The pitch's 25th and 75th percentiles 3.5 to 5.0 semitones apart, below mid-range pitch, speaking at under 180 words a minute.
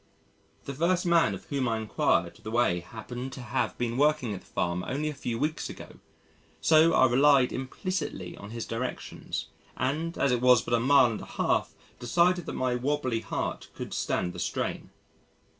No: average, 4.4 semitones; low, 125 Hz; average, 185 wpm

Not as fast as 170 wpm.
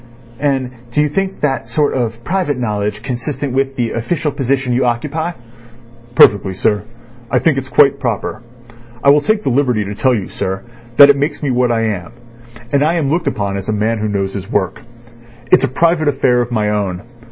No: average, 200 wpm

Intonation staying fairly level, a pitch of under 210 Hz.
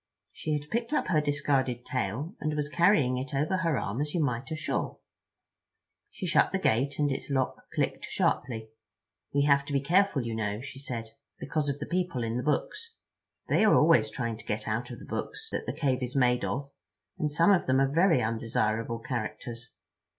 No: average, 4.2 semitones; low, 135 Hz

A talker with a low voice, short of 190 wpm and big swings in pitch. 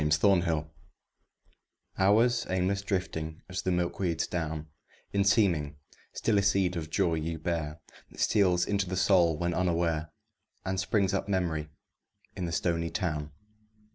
No: very low, 90 Hz; average, 140 wpm; average, 3.0 semitones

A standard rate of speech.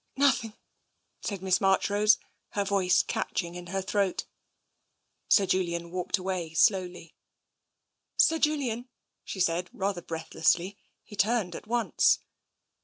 No: slow, 130 wpm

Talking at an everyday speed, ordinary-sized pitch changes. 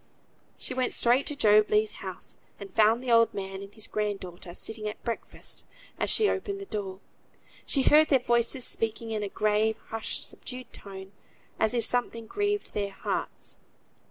Yes: average, 175 wpm; average, 3.3 semitones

